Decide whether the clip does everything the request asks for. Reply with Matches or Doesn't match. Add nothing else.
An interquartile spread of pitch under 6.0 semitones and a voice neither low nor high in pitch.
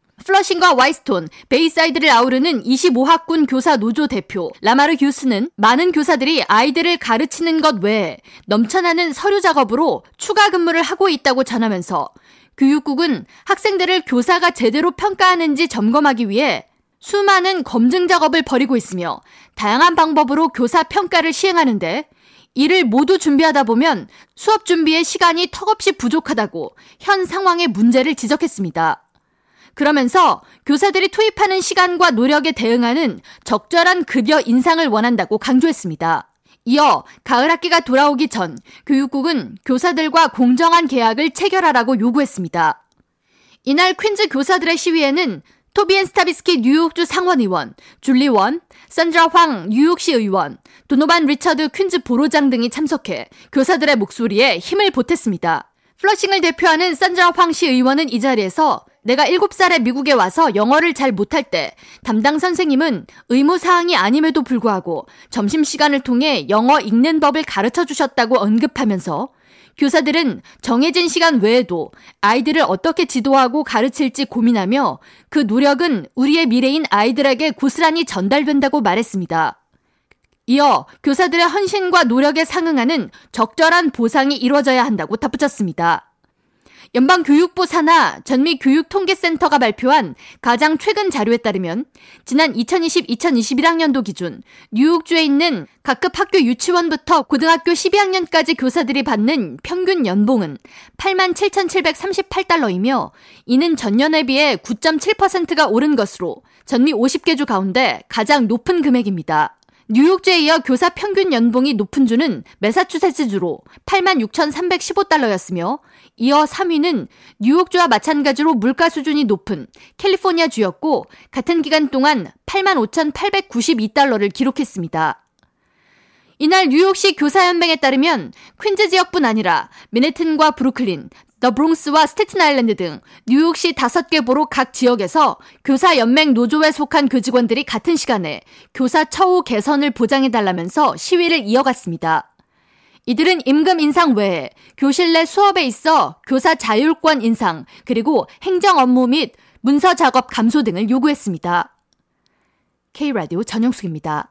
Doesn't match